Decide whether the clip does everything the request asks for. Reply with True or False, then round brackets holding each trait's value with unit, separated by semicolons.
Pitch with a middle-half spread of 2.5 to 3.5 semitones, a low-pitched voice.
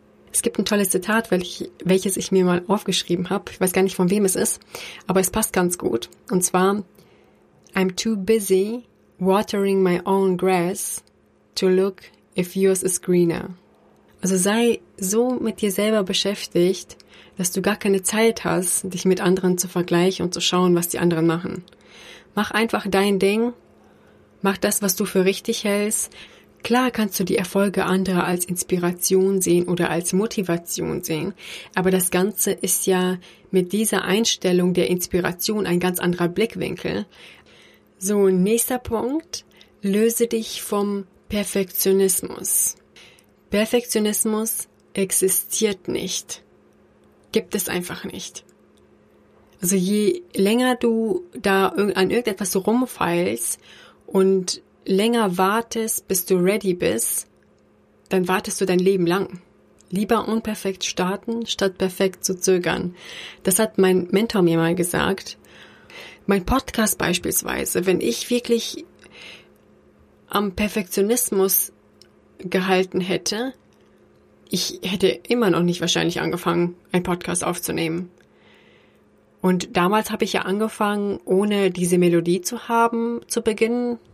False (2.8 semitones; 190 Hz)